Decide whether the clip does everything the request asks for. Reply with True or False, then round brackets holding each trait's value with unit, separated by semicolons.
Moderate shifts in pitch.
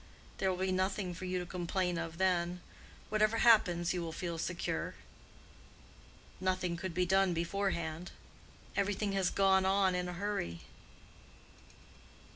False (1.9 semitones)